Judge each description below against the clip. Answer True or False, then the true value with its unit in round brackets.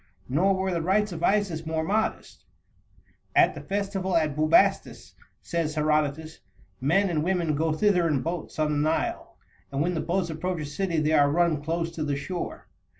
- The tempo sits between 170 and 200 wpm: True (180 wpm)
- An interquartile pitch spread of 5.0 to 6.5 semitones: False (3.2 semitones)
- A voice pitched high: False (165 Hz)